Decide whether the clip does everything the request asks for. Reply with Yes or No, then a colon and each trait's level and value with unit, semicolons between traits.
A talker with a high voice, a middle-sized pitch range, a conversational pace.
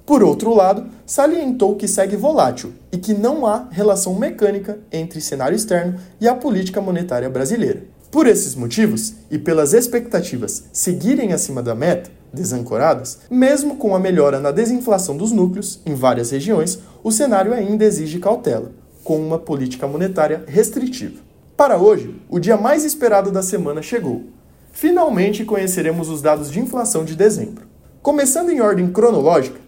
No: high, 205 Hz; wide, 5.8 semitones; average, 150 wpm